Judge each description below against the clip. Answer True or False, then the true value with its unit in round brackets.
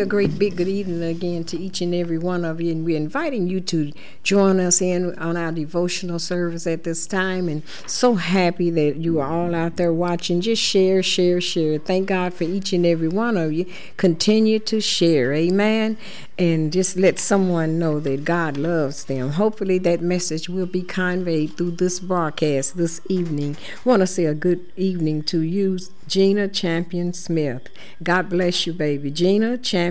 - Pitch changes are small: True (2.1 semitones)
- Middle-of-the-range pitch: True (175 Hz)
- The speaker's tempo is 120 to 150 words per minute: False (185 wpm)